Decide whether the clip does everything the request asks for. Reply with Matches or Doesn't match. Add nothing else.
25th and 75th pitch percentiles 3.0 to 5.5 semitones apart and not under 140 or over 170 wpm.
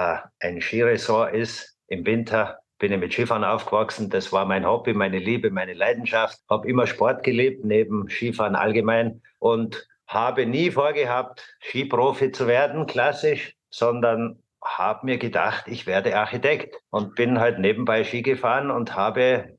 Doesn't match